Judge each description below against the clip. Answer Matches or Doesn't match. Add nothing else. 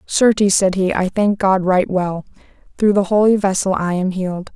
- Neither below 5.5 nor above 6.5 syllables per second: Doesn't match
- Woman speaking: Matches